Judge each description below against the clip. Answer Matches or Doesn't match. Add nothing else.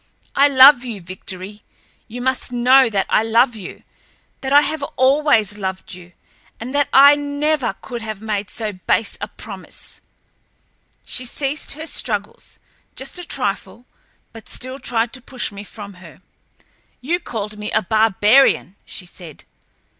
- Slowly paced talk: Doesn't match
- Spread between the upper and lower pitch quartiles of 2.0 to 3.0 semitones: Doesn't match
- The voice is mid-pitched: Doesn't match